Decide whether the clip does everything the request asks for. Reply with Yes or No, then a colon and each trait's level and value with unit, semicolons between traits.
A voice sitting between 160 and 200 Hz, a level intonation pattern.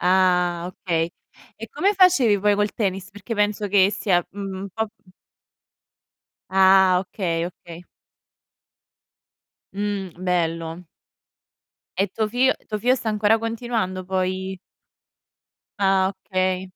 Yes: high, 190 Hz; narrow, 2.3 semitones